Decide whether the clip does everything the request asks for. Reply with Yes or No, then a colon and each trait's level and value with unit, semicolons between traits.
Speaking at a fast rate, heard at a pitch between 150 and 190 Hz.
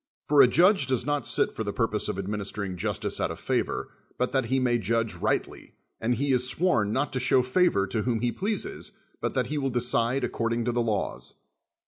No: fast, 210 wpm; low, 120 Hz